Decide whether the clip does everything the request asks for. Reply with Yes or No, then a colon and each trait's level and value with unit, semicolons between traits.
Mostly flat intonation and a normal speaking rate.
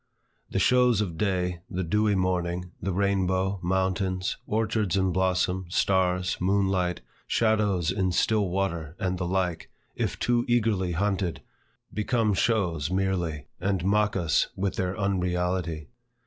No: narrow, 2.0 semitones; slow, 130 wpm